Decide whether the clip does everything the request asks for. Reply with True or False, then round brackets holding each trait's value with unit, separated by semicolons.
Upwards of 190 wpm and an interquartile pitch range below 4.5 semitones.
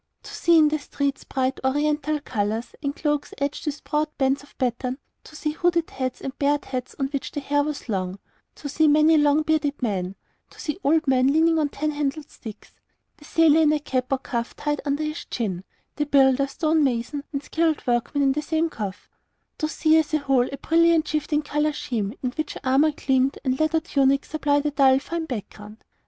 True (200 wpm; 2.6 semitones)